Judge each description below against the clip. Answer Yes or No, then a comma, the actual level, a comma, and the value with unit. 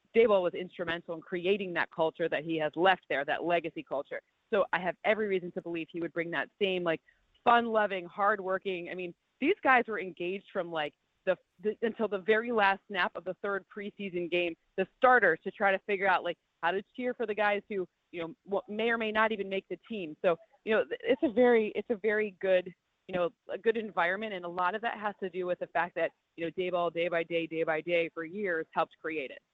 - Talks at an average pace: No, fast, 235 wpm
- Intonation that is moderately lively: Yes, average, 3.8 semitones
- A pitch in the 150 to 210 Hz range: Yes, high, 190 Hz